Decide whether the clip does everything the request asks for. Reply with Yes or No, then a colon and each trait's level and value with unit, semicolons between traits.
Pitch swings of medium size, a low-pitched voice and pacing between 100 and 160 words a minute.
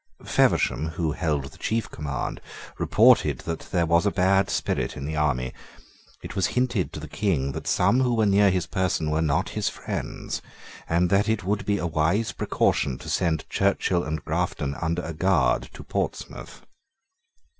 No: average, 4.3 semitones; very low, 85 Hz; average, 175 wpm